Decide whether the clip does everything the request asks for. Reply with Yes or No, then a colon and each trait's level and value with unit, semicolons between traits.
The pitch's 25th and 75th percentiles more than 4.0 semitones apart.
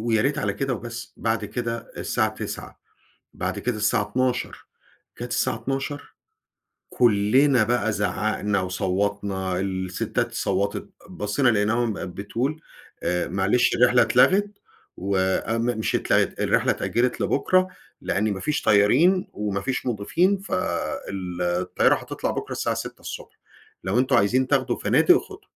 Yes: average, 4.4 semitones